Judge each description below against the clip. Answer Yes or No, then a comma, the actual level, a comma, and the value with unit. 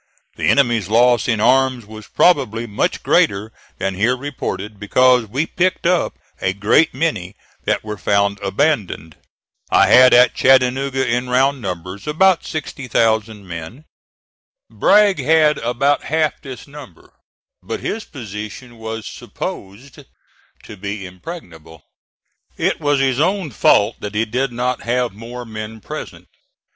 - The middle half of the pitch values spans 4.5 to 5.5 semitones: Yes, average, 4.8 semitones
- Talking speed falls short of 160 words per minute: Yes, slow, 135 wpm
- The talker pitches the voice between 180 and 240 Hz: No, low, 120 Hz